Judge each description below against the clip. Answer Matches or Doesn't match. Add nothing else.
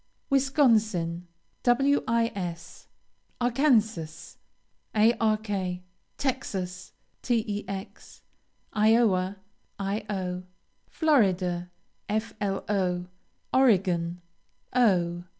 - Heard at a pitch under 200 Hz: Doesn't match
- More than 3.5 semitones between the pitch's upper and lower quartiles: Matches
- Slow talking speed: Matches